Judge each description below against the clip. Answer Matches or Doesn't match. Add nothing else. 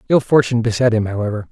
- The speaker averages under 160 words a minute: Doesn't match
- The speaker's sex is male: Matches